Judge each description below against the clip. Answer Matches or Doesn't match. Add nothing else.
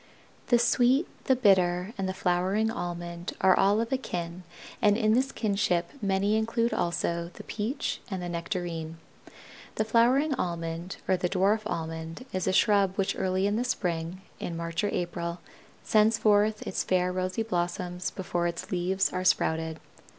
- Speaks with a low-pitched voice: Doesn't match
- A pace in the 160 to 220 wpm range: Matches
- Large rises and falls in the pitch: Doesn't match